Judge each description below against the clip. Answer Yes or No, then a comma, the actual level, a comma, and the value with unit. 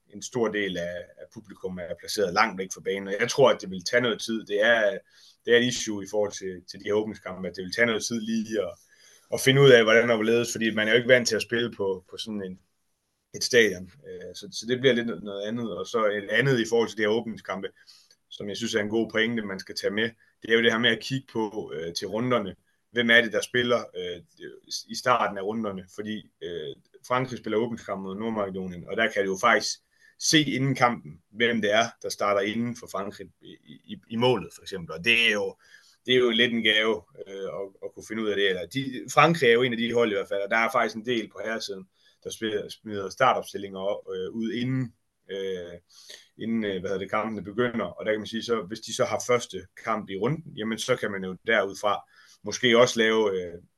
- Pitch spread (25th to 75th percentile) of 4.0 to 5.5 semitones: No, average, 3.6 semitones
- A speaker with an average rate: No, fast, 245 wpm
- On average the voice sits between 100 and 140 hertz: Yes, low, 115 Hz